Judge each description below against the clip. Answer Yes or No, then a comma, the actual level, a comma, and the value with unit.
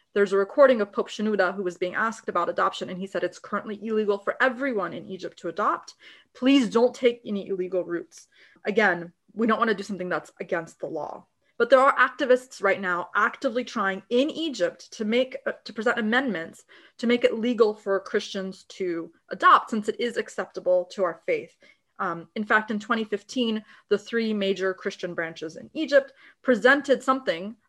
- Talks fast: No, average, 185 wpm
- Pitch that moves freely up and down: No, average, 4.6 semitones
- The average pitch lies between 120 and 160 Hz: No, high, 215 Hz